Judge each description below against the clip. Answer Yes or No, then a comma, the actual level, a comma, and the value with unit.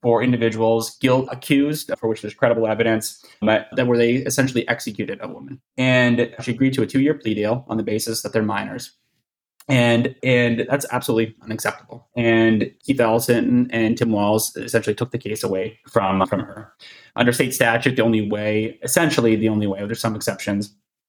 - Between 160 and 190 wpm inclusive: Yes, average, 180 wpm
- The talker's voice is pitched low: Yes, low, 115 Hz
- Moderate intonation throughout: No, narrow, 2.2 semitones